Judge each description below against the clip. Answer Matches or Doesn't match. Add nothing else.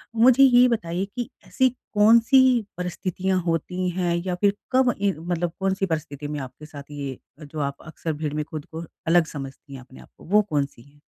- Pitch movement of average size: Doesn't match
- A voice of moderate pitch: Matches